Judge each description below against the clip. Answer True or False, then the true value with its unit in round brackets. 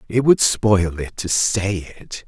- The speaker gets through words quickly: False (185 wpm)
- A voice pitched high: False (100 Hz)